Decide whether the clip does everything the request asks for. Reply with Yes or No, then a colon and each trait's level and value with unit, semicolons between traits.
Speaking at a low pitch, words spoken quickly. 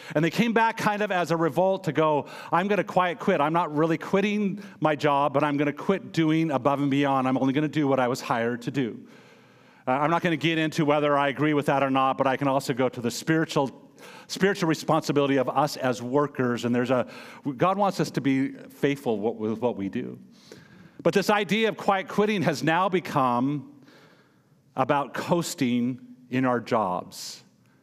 No: medium, 150 Hz; fast, 210 wpm